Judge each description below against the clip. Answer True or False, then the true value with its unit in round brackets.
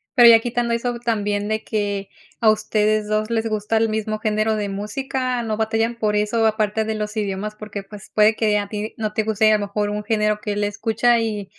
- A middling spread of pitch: False (1.1 semitones)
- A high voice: True (215 Hz)